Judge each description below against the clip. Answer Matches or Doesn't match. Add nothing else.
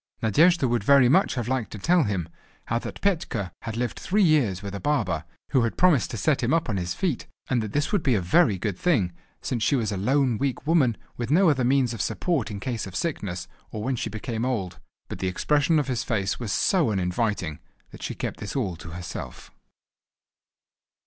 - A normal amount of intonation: Doesn't match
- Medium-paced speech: Doesn't match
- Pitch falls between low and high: Doesn't match